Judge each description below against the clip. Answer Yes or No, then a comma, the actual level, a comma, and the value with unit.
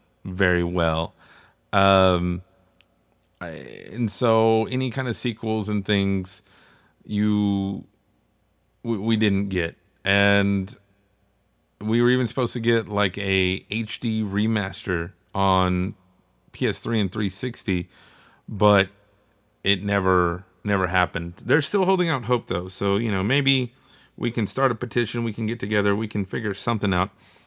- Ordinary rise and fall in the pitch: Yes, average, 3.2 semitones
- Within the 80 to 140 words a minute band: Yes, slow, 135 wpm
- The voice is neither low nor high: No, low, 100 Hz